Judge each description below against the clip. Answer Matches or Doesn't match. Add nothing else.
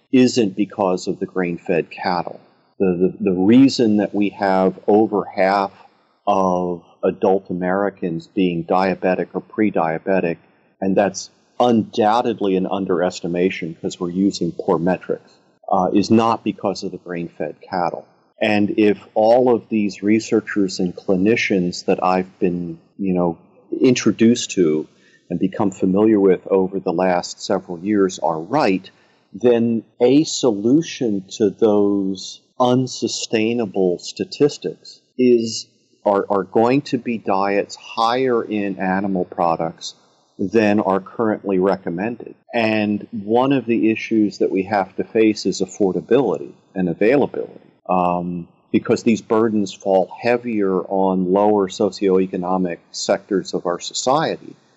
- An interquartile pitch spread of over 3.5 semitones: Doesn't match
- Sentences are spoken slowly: Matches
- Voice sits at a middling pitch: Doesn't match